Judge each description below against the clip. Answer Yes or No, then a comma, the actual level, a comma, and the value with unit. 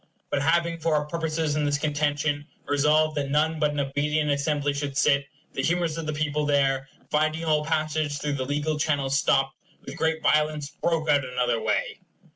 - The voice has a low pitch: No, medium, 150 Hz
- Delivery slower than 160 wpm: No, average, 185 wpm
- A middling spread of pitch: No, narrow, 1.5 semitones